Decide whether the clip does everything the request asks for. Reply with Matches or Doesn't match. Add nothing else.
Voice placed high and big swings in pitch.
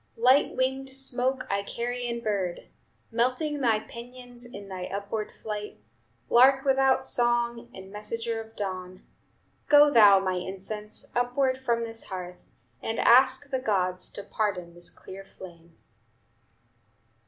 Doesn't match